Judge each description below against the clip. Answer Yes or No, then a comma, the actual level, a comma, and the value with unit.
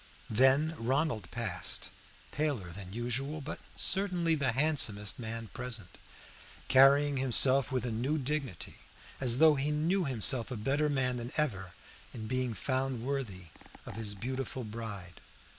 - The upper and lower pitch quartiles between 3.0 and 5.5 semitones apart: Yes, average, 4.1 semitones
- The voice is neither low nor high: No, low, 130 Hz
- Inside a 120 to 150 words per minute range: Yes, average, 140 wpm